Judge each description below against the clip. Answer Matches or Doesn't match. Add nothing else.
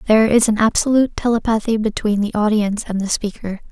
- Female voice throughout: Matches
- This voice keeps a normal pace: Matches